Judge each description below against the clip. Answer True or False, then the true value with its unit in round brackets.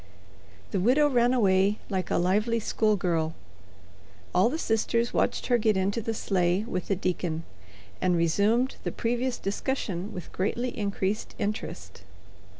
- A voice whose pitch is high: True (205 Hz)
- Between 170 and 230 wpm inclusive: False (140 wpm)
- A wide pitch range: False (4.1 semitones)